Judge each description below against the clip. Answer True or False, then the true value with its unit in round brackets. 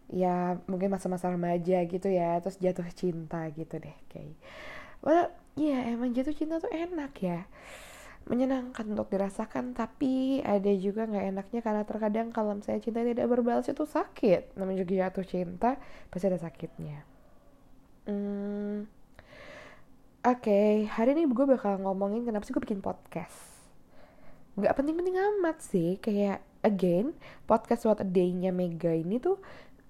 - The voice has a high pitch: True (205 Hz)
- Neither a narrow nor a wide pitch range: True (4.9 semitones)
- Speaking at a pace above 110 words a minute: True (140 wpm)